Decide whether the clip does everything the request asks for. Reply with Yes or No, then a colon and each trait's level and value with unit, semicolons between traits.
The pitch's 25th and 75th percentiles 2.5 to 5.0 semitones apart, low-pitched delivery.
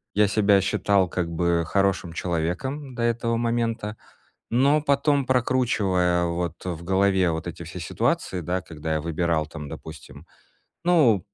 No: wide, 5.6 semitones; very low, 95 Hz